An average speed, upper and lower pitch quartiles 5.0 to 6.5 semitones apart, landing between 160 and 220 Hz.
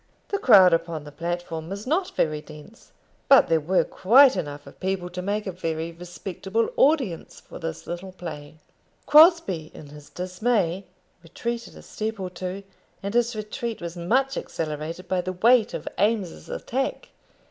Yes: average, 160 wpm; wide, 5.5 semitones; medium, 185 Hz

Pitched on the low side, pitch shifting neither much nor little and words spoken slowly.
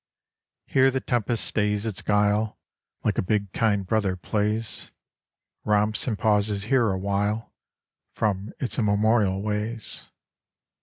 No: low, 105 Hz; narrow, 1.5 semitones; slow, 115 wpm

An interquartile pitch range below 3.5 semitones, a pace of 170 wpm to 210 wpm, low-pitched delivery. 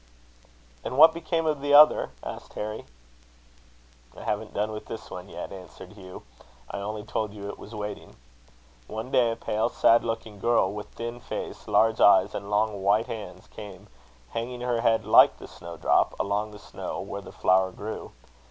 Yes: narrow, 2.4 semitones; average, 175 wpm; low, 110 Hz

